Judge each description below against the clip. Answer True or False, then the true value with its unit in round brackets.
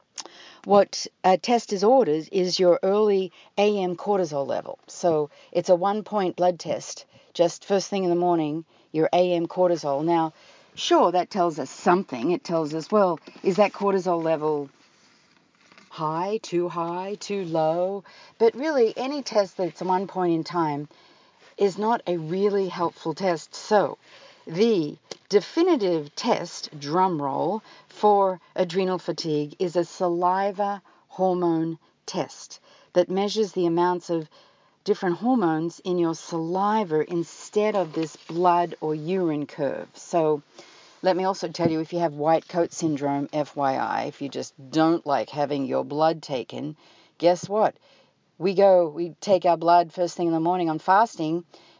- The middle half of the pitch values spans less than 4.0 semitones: True (3.3 semitones)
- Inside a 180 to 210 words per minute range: False (150 wpm)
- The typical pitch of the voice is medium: True (175 Hz)